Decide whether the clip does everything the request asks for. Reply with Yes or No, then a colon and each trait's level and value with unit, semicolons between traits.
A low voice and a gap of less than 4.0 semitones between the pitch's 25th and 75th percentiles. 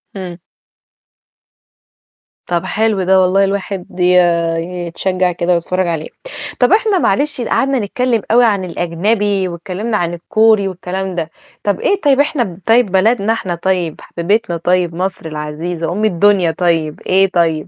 No: medium, 185 Hz; average, 3.6 semitones